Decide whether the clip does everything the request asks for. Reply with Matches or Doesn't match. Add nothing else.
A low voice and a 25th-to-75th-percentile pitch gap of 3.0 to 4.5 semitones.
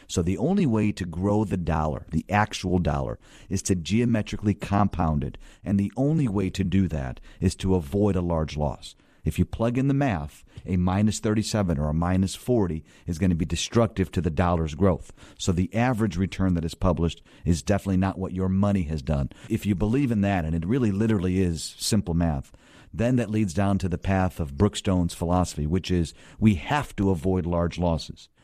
Matches